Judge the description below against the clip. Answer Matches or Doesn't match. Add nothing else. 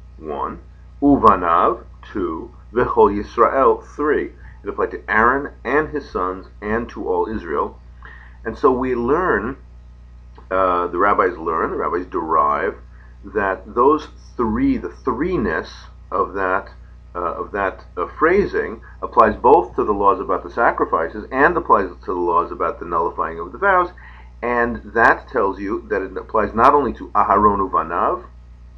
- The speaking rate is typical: Matches